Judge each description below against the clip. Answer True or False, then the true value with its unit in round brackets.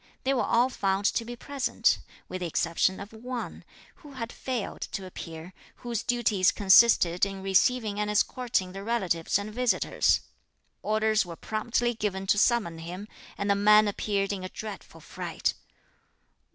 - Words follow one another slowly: False (155 wpm)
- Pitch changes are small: False (3.7 semitones)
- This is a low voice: False (210 Hz)